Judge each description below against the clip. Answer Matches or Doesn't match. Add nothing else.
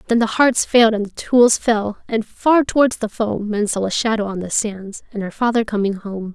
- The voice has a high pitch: Matches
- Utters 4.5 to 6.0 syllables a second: Matches